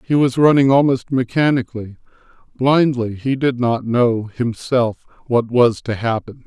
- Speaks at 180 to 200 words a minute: No, average, 140 wpm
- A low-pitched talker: Yes, low, 125 Hz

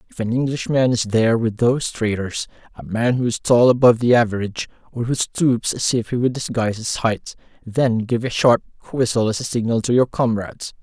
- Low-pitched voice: Yes, low, 120 Hz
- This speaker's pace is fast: Yes, fast, 210 wpm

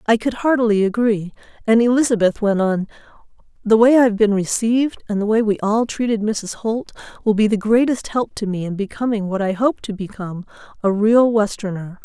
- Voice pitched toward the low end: No, high, 215 Hz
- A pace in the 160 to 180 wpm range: No, average, 195 wpm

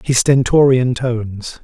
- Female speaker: No, male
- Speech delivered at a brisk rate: No, slow, 110 wpm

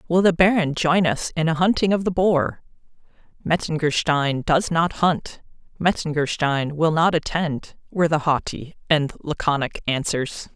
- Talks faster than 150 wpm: No, slow, 135 wpm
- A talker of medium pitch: Yes, medium, 160 Hz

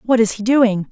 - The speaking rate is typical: No, fast, 265 wpm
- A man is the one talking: No, female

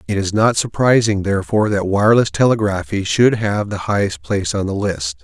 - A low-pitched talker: Yes, low, 105 Hz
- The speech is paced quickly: No, average, 185 wpm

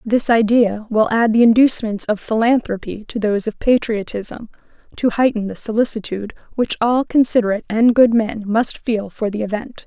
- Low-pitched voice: No, high, 220 Hz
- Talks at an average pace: Yes, average, 165 wpm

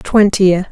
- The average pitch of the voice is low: No, high, 195 Hz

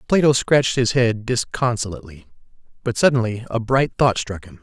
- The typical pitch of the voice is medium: No, low, 120 Hz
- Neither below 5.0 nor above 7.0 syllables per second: Yes, 5.4 syllables/s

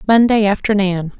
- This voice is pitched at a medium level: No, high, 205 Hz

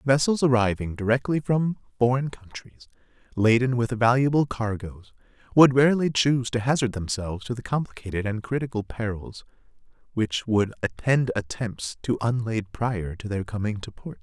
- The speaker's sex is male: Yes, male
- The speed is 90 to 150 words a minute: Yes, average, 145 wpm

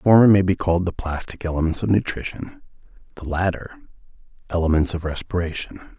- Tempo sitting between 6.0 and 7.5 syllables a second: Yes, 6.3 syllables/s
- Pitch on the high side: No, very low, 85 Hz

